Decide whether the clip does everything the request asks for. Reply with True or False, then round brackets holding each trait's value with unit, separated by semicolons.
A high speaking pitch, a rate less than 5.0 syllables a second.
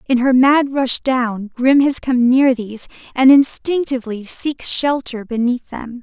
True (255 Hz; 4.1 syllables/s)